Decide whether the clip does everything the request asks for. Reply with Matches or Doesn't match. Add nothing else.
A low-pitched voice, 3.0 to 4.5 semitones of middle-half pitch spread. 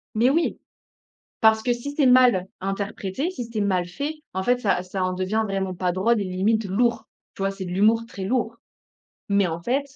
Doesn't match